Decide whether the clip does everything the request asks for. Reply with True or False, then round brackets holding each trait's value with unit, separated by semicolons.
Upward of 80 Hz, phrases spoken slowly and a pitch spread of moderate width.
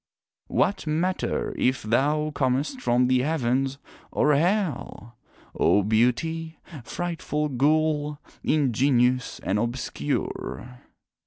True (140 Hz; 90 wpm; 3.9 semitones)